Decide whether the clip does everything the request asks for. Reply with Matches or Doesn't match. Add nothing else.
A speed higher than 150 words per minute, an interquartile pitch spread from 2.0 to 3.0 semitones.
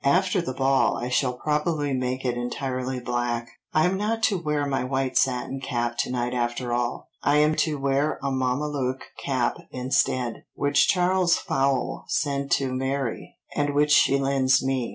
Matches